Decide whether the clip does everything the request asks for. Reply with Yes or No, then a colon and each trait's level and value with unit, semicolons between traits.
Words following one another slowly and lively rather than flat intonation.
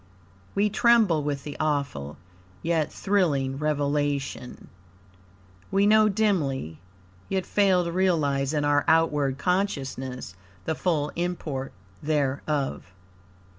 No: slow, 100 wpm; average, 4.7 semitones